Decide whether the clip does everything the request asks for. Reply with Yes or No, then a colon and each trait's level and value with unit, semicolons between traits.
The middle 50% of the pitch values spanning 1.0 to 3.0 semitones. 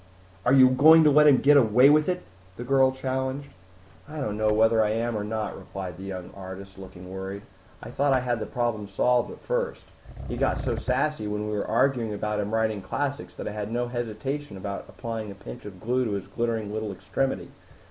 No: average, 4.4 semitones